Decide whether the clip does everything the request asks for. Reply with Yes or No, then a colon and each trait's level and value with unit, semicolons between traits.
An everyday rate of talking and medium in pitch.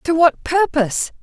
No: average, 145 wpm; very high, 310 Hz